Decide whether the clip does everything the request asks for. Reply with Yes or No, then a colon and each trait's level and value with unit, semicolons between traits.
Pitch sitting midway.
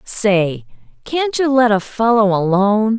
No: high, 215 Hz